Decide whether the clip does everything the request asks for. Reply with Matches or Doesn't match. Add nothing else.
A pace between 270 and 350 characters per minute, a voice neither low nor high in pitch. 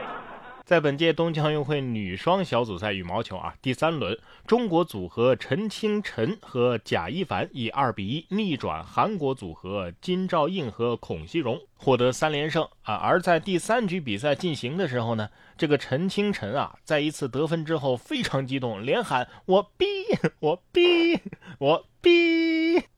Doesn't match